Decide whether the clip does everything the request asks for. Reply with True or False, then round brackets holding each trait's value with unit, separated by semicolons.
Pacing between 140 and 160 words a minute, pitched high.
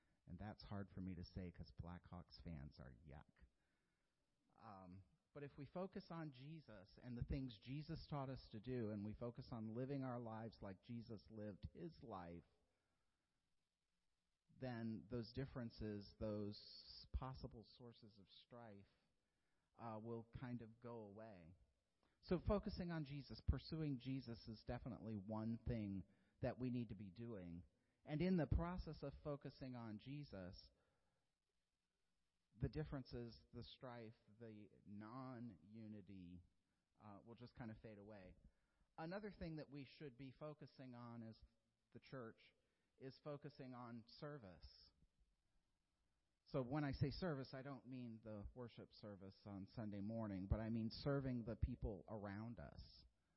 False (145 wpm; 115 Hz)